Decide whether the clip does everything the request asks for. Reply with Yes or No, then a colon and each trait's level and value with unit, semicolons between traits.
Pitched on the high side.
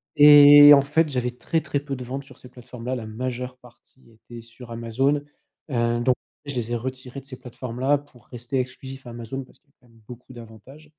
No: low, 125 Hz